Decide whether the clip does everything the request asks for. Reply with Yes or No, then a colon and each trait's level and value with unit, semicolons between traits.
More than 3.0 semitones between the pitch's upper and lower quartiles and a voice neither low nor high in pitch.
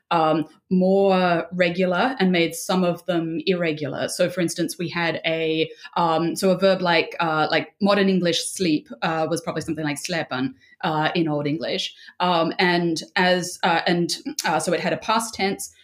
No: narrow, 2.5 semitones; medium, 170 Hz